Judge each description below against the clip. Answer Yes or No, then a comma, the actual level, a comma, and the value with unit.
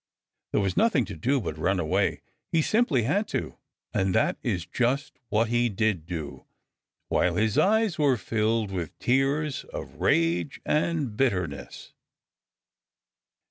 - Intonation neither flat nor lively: No, wide, 7.1 semitones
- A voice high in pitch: No, low, 115 Hz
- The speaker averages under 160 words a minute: Yes, average, 140 wpm